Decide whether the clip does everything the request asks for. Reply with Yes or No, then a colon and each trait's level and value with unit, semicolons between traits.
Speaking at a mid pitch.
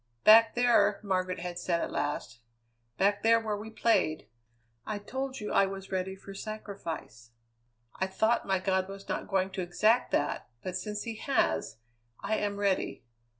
No: high, 195 Hz